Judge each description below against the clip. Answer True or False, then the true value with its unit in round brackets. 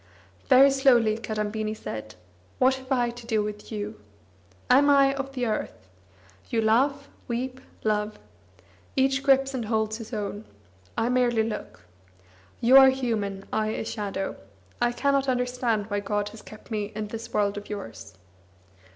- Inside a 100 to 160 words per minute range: True (150 wpm)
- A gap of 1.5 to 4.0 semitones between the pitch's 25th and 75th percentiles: True (3.6 semitones)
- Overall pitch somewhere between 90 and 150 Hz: False (225 Hz)